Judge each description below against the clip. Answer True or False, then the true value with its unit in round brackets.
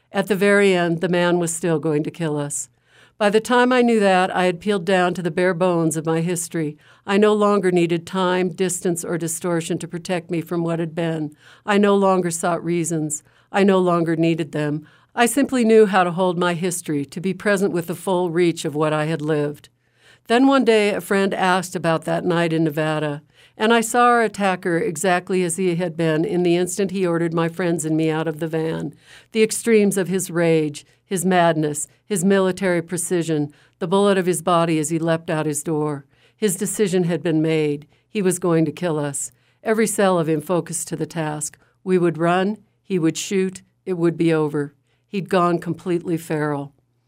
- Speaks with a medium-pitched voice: True (175 Hz)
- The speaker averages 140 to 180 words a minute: False (205 wpm)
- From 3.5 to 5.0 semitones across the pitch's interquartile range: False (3.0 semitones)